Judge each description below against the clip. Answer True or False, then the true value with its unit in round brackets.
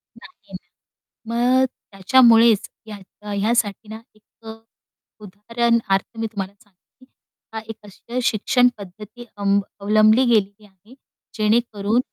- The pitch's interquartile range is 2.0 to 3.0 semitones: True (2.6 semitones)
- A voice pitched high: True (215 Hz)